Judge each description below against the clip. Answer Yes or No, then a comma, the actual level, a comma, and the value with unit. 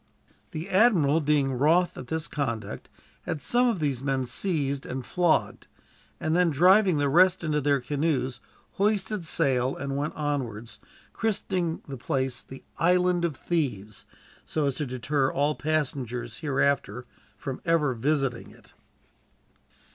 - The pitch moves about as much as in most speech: Yes, average, 4.2 semitones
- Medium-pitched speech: Yes, medium, 145 Hz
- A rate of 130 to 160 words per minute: Yes, average, 140 wpm